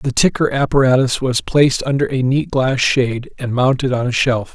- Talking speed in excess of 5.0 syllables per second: Yes, 5.2 syllables/s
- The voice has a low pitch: Yes, low, 130 Hz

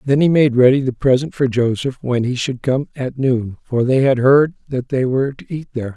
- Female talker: No, male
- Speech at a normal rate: No, fast, 240 wpm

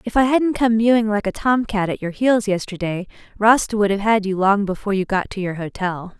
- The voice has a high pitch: Yes, high, 205 Hz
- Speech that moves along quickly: Yes, fast, 240 wpm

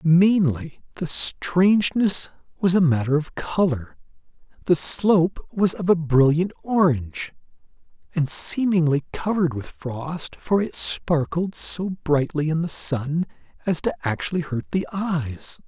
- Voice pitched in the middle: Yes, medium, 165 Hz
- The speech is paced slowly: Yes, slow, 130 wpm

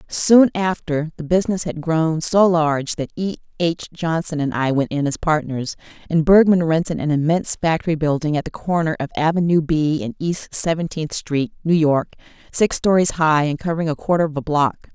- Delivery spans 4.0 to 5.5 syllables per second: Yes, 5.3 syllables/s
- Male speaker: No, female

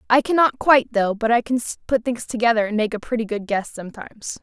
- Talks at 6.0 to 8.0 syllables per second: Yes, 6.3 syllables/s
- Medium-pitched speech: No, high, 230 Hz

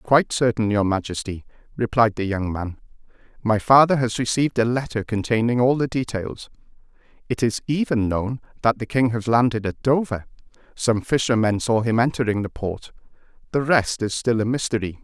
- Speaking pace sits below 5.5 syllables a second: Yes, 5.3 syllables/s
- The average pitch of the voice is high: No, low, 115 Hz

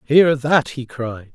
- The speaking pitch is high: No, low, 135 Hz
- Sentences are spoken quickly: No, average, 180 wpm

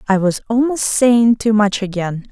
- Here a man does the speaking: No, female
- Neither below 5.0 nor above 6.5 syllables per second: No, 4.4 syllables/s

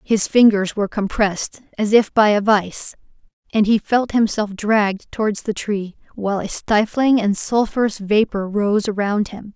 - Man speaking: No, female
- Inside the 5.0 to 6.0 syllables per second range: No, 4.6 syllables/s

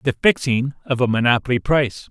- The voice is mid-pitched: No, low, 125 Hz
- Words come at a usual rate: Yes, average, 170 wpm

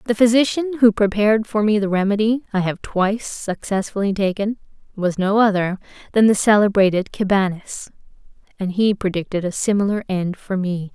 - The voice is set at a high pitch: Yes, high, 205 Hz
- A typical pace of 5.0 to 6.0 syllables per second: Yes, 5.3 syllables/s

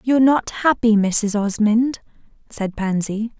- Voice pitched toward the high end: Yes, high, 225 Hz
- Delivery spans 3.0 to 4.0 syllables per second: Yes, 3.9 syllables/s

